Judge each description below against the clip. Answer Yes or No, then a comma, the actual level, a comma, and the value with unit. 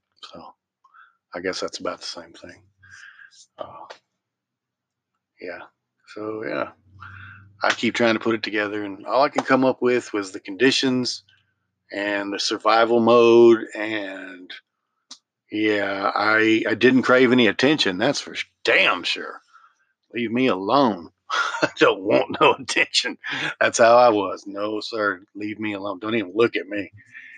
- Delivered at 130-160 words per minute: Yes, average, 145 wpm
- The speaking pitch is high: No, low, 110 Hz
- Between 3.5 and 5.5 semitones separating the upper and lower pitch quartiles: No, average, 2.7 semitones